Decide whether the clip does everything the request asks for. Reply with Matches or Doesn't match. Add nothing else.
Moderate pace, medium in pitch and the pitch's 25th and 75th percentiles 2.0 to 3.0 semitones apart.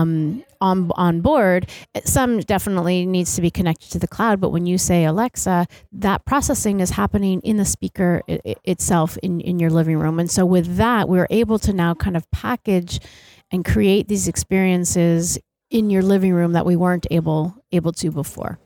Matches